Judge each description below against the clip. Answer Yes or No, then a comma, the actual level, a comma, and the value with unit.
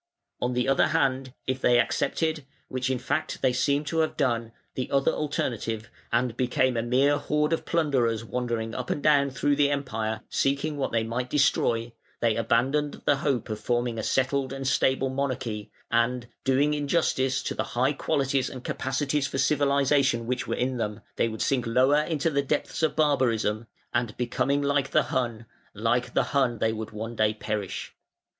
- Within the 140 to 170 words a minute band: No, average, 180 wpm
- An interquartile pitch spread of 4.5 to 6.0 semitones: No, average, 3.2 semitones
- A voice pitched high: No, low, 130 Hz